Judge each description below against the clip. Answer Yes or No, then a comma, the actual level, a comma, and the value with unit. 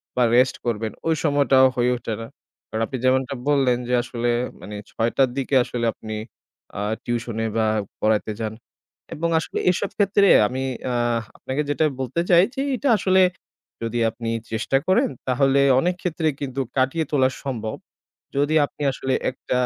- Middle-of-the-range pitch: No, low, 130 Hz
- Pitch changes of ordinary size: Yes, average, 3.8 semitones